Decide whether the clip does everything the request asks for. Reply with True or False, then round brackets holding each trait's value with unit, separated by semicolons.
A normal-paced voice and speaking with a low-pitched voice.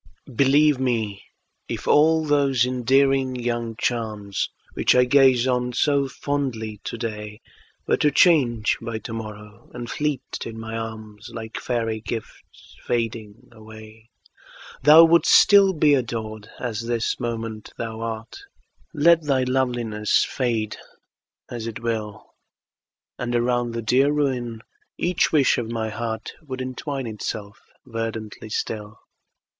False (130 wpm; 120 Hz)